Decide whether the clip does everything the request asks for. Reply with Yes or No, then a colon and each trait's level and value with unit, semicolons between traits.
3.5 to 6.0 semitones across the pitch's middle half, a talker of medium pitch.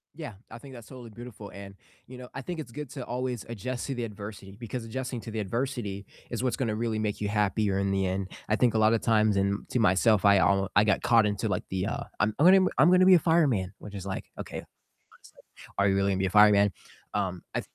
No: average, 3.9 semitones; low, 110 Hz